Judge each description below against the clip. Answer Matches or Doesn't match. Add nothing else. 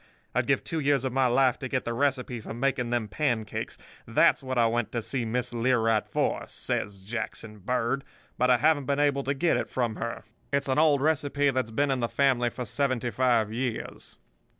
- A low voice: Matches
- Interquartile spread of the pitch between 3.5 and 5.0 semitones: Doesn't match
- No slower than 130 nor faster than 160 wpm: Doesn't match